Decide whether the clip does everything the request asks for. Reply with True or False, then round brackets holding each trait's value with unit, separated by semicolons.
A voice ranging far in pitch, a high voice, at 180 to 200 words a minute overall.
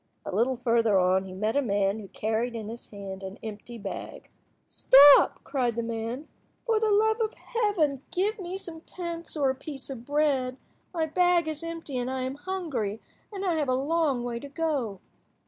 True (6.5 semitones; 265 Hz; 190 wpm)